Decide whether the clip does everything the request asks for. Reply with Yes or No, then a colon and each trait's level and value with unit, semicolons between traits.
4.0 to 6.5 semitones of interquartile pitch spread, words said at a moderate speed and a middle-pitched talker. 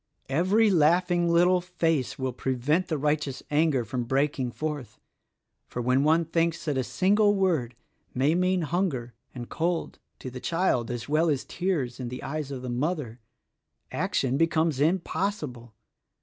Yes: average, 5.2 semitones; average, 150 wpm; medium, 150 Hz